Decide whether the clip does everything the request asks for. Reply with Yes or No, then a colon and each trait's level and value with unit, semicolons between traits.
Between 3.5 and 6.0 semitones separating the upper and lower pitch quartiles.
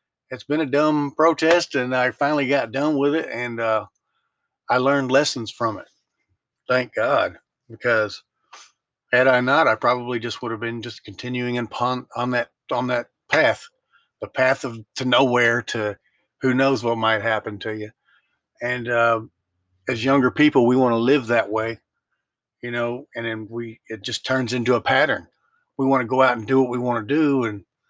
No: average, 2.7 semitones